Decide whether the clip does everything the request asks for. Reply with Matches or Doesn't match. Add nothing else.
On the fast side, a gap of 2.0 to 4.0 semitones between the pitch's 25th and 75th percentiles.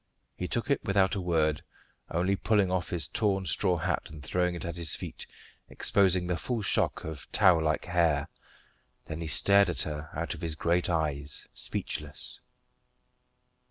Doesn't match